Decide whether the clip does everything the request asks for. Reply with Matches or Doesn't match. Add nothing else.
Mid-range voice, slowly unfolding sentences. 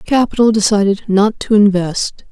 Doesn't match